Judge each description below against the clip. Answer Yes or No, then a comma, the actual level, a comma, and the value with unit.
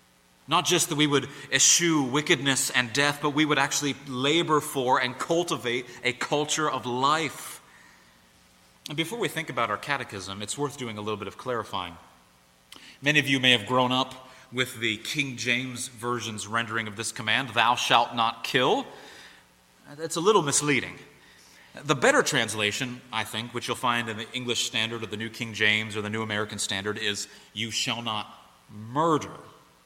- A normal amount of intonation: Yes, average, 4.6 semitones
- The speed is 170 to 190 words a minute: Yes, average, 175 wpm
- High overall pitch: No, low, 120 Hz